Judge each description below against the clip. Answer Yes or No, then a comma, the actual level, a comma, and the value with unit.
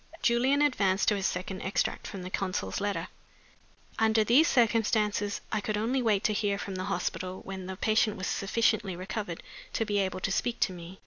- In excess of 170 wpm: Yes, average, 190 wpm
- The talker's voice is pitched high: Yes, high, 205 Hz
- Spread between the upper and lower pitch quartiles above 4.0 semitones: No, average, 2.8 semitones